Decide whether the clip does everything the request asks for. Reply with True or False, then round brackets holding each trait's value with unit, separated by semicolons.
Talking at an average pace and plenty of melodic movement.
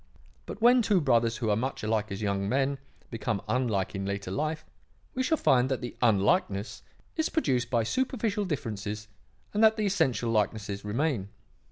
True (170 wpm; 7.6 semitones)